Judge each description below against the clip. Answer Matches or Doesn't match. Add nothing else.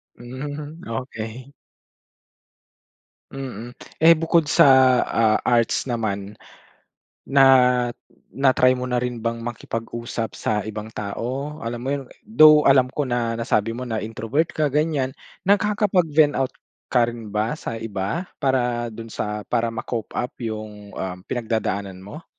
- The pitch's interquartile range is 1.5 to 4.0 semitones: Matches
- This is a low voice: Matches